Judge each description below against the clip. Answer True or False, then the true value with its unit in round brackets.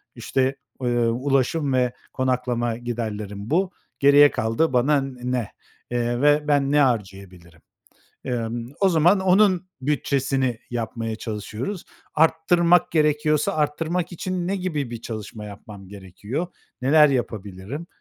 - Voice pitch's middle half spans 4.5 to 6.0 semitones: True (5.1 semitones)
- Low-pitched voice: True (130 Hz)